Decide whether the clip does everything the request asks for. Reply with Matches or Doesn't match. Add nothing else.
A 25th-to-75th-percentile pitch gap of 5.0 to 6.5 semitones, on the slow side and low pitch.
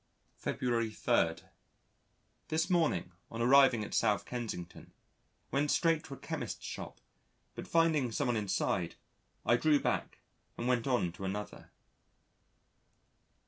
Matches